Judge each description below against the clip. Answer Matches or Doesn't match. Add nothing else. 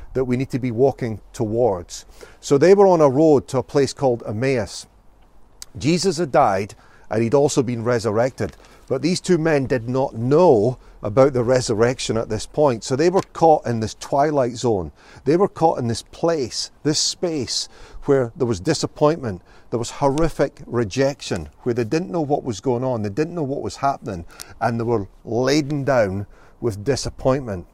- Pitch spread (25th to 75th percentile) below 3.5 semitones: Doesn't match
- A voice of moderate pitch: Doesn't match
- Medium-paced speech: Matches